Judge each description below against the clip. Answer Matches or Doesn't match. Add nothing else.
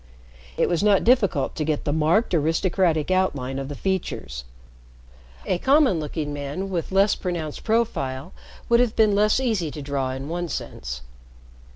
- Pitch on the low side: Doesn't match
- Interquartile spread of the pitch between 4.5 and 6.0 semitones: Matches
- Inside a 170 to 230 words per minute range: Doesn't match